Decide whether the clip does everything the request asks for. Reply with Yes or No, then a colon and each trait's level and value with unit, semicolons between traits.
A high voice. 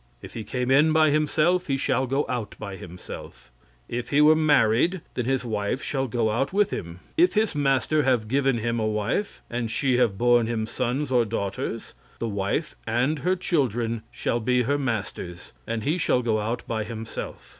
No: low, 125 Hz